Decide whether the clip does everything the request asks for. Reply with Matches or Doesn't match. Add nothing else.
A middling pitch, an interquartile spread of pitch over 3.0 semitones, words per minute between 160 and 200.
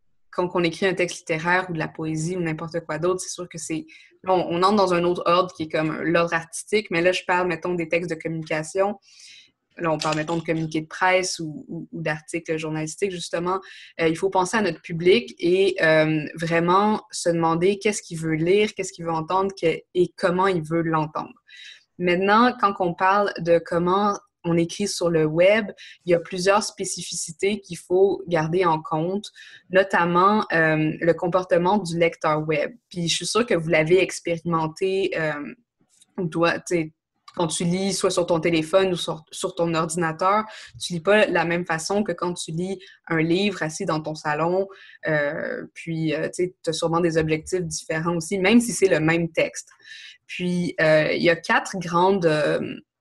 Doesn't match